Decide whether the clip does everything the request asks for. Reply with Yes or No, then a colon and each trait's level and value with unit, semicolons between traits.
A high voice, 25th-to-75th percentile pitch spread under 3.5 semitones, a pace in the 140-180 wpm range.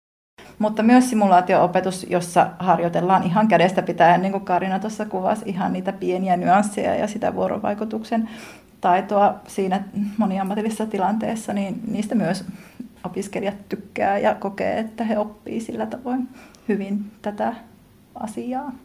No: high, 200 Hz; average, 2.8 semitones; average, 125 wpm